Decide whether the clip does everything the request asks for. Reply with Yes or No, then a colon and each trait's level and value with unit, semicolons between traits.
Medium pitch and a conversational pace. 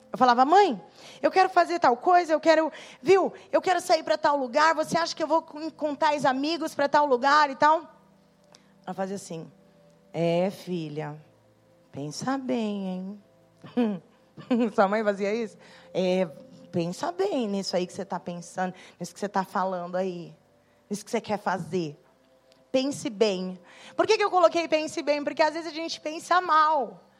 No: high, 230 Hz; average, 170 wpm